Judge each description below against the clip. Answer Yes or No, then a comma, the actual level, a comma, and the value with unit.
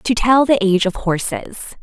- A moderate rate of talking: Yes, average, 195 wpm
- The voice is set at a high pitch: Yes, high, 210 Hz